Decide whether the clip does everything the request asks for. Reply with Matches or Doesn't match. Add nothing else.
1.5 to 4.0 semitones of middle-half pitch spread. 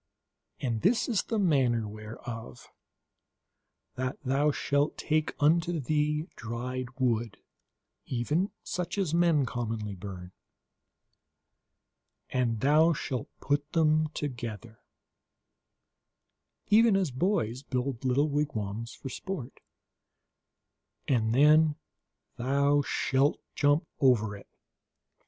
Doesn't match